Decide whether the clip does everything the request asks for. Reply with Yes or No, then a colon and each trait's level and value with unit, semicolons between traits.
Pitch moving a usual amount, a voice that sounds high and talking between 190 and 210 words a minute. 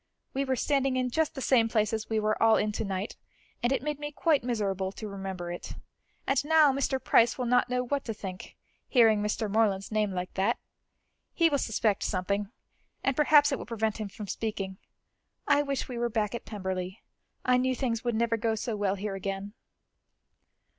Yes: average, 4.2 semitones; high, 225 Hz; average, 200 wpm